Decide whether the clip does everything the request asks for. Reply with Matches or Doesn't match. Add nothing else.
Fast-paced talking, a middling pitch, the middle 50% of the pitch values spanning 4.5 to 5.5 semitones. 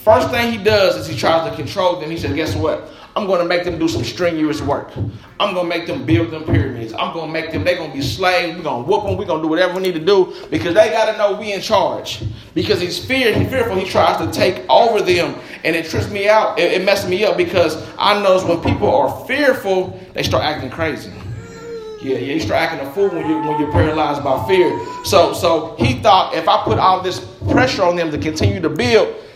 Matches